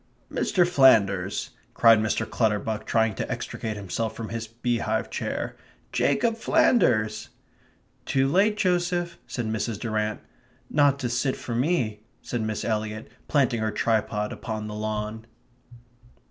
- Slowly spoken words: Yes, slow, 130 wpm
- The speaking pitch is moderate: No, low, 110 Hz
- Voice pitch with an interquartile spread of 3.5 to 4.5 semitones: Yes, average, 3.8 semitones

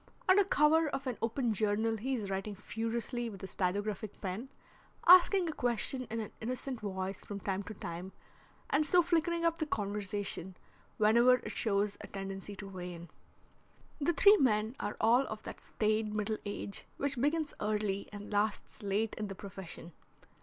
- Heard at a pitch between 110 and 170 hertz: No, high, 215 Hz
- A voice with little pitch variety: No, average, 4.5 semitones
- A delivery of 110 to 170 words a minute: Yes, average, 165 wpm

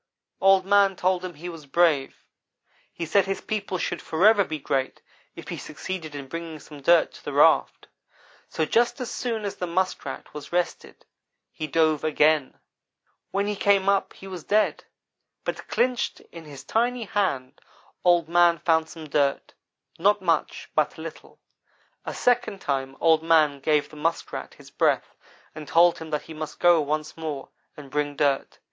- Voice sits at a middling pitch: Yes, medium, 165 Hz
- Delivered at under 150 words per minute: No, average, 170 wpm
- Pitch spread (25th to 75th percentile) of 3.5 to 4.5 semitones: Yes, average, 4.0 semitones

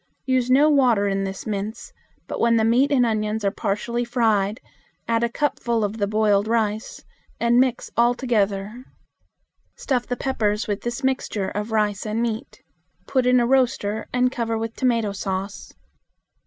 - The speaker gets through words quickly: No, average, 165 wpm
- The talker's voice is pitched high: Yes, high, 230 Hz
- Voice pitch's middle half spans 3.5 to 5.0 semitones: No, average, 2.9 semitones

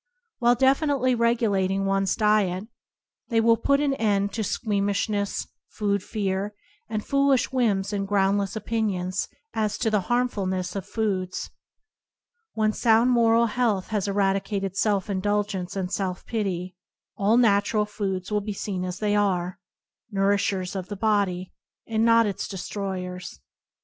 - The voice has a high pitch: Yes, high, 205 Hz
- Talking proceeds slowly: No, average, 145 wpm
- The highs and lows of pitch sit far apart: No, narrow, 2.5 semitones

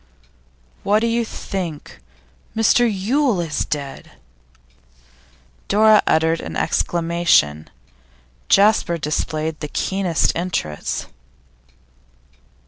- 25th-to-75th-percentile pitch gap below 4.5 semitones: No, average, 5.2 semitones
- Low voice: No, medium, 175 Hz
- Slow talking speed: Yes, slow, 80 wpm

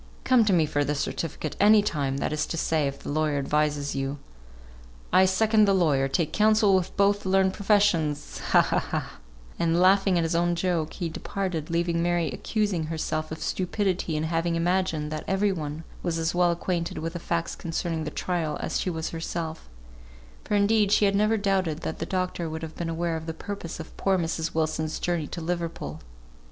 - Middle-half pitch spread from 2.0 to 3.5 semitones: Yes, average, 3.1 semitones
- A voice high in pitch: No, medium, 170 Hz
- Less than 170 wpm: No, average, 200 wpm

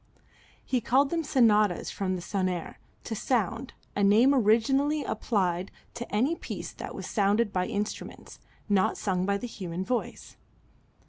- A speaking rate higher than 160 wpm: No, average, 140 wpm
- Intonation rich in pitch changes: No, average, 4.6 semitones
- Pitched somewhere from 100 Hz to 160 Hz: No, high, 210 Hz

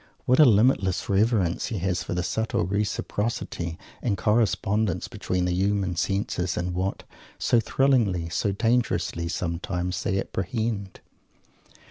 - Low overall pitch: Yes, very low, 95 Hz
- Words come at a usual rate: No, slow, 125 wpm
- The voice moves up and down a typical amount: Yes, average, 3.6 semitones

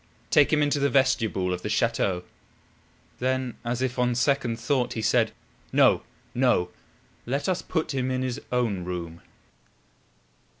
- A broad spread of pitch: No, average, 3.3 semitones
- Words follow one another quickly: No, average, 145 wpm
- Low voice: Yes, low, 125 Hz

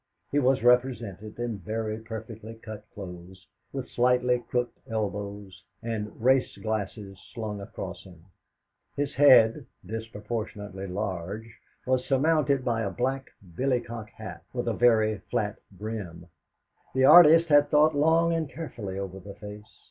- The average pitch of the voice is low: Yes, low, 110 Hz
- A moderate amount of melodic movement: Yes, average, 4.0 semitones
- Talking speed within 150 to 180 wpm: No, slow, 135 wpm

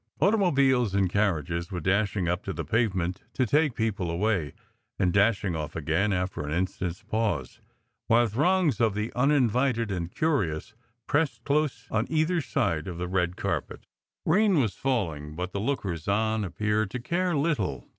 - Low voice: Yes, low, 105 Hz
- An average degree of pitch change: No, wide, 6.7 semitones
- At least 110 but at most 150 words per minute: No, average, 165 wpm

